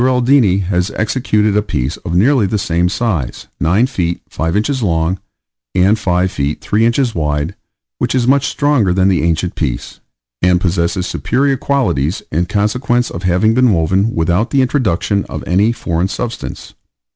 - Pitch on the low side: Yes, very low, 95 Hz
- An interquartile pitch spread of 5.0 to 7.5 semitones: Yes, wide, 5.6 semitones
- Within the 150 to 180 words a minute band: Yes, average, 160 wpm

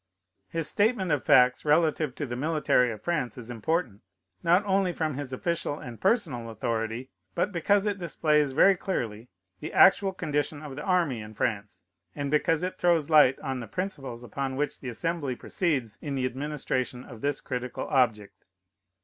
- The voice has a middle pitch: Yes, medium, 145 Hz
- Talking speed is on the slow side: No, average, 170 wpm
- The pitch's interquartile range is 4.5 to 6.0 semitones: Yes, average, 5.3 semitones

